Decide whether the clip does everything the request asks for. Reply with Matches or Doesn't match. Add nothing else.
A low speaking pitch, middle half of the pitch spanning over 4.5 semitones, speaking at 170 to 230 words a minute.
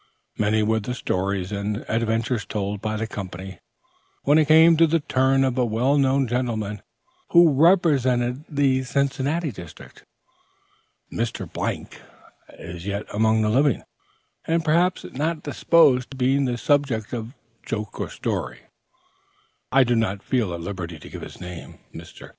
Doesn't match